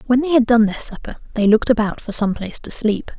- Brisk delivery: Yes, fast, 265 wpm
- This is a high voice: Yes, high, 225 Hz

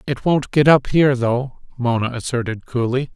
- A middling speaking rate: Yes, average, 170 wpm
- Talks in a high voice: No, low, 130 Hz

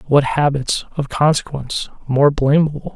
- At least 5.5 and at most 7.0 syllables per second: No, 4.8 syllables/s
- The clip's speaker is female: No, male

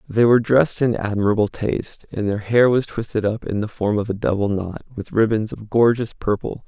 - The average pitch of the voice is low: Yes, low, 110 Hz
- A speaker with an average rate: No, fast, 215 wpm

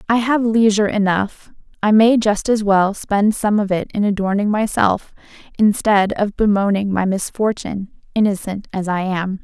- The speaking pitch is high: Yes, high, 205 Hz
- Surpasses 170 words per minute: No, average, 155 wpm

